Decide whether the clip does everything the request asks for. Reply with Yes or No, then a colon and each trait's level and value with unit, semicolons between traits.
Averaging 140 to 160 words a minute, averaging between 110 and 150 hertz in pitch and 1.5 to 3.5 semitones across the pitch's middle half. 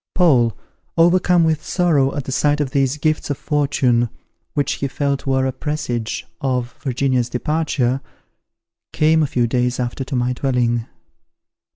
Yes: average, 150 wpm; low, 135 Hz; average, 3.2 semitones